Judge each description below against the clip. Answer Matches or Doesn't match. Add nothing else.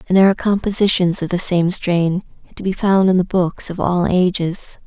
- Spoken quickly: Matches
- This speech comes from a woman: Matches